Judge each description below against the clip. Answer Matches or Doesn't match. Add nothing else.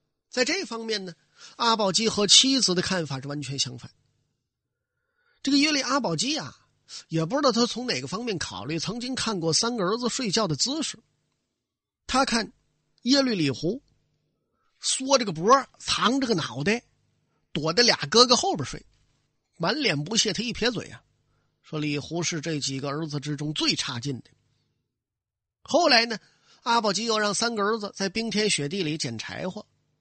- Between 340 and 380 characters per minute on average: Doesn't match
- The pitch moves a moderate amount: Doesn't match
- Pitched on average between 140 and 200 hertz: Matches